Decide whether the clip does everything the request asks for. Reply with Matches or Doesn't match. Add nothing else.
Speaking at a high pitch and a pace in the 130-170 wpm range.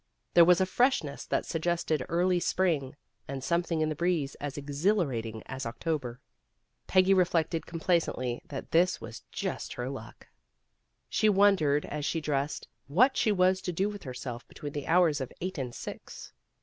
Doesn't match